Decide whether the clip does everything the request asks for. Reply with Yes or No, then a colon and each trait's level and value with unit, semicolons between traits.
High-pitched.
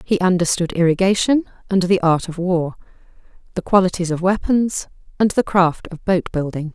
No: medium, 180 Hz